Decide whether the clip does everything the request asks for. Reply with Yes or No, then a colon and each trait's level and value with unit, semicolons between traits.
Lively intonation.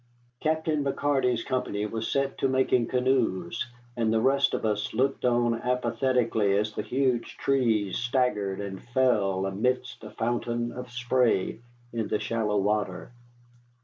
No: average, 3.4 semitones